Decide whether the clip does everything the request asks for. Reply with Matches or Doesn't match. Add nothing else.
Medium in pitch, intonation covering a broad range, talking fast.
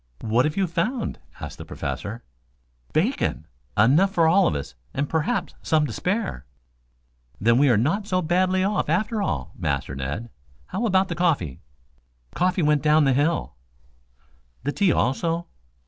Doesn't match